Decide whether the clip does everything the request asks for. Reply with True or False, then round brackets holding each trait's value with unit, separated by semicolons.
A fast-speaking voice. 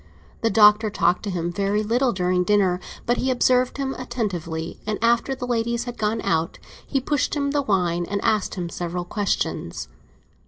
False (180 wpm)